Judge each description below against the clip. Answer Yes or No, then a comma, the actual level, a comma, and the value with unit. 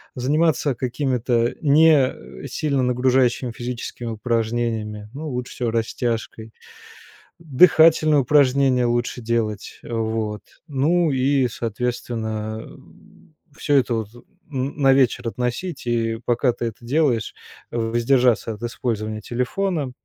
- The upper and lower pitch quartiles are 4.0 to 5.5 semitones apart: No, average, 3.2 semitones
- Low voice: Yes, low, 125 Hz